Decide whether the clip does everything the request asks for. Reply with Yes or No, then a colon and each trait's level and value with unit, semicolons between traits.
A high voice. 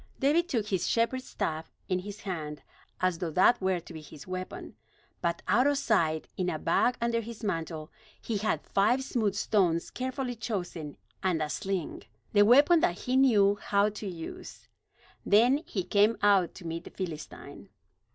Yes: high, 200 Hz